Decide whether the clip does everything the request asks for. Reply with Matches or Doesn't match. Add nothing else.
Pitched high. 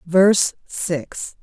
Doesn't match